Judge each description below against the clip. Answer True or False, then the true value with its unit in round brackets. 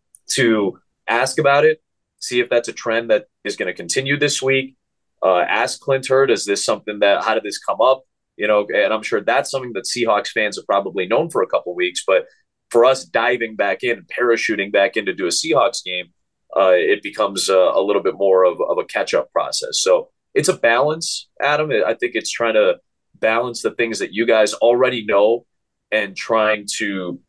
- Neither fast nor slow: False (210 wpm)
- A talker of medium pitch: True (145 Hz)